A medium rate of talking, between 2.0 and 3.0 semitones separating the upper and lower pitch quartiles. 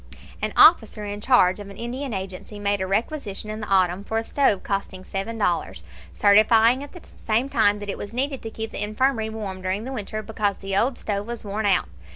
No: fast, 215 wpm; narrow, 2.5 semitones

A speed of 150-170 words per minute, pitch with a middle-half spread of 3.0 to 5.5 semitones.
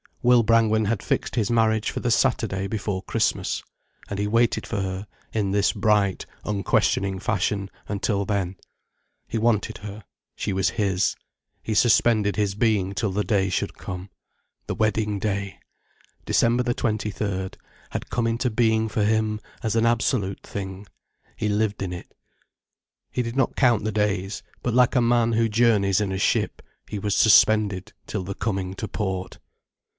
No: average, 165 wpm; narrow, 2.4 semitones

